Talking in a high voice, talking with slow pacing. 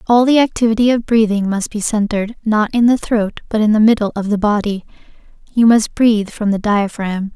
No: high, 215 Hz; average, 195 wpm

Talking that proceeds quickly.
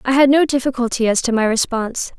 Yes: fast, 220 wpm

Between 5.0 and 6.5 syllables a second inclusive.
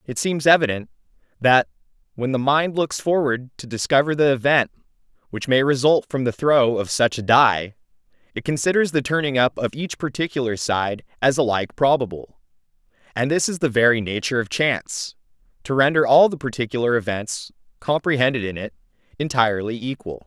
Yes: 5.5 syllables/s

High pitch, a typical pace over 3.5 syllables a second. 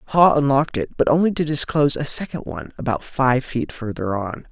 No: low, 135 Hz; 5.5 syllables/s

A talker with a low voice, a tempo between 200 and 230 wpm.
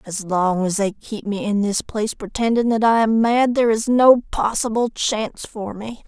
No: high, 215 Hz; fast, 205 wpm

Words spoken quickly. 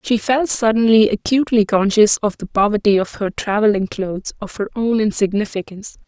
No: average, 160 wpm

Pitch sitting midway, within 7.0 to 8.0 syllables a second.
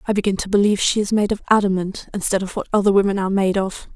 No: high, 200 Hz; 7.2 syllables/s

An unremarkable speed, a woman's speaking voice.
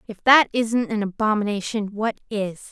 Yes: average, 155 wpm; female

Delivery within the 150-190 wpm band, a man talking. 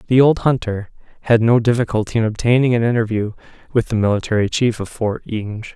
Yes: average, 175 wpm; male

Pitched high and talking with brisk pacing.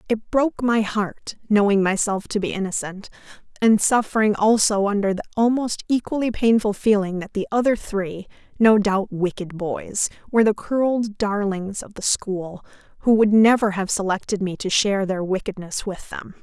No: high, 205 Hz; average, 155 wpm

